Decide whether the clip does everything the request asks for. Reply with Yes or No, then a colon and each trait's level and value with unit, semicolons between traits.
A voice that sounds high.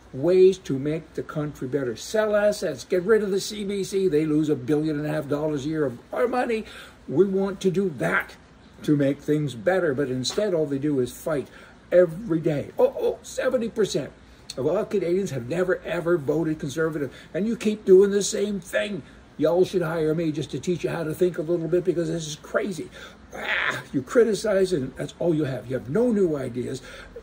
No: medium, 170 Hz